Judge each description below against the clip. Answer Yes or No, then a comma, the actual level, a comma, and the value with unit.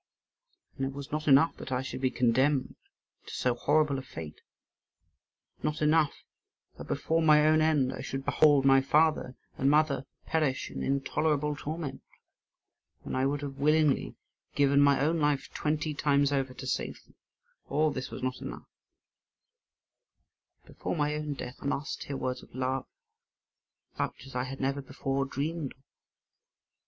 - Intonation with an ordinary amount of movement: No, narrow, 2.1 semitones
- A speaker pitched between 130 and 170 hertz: Yes, medium, 140 Hz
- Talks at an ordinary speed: Yes, average, 160 wpm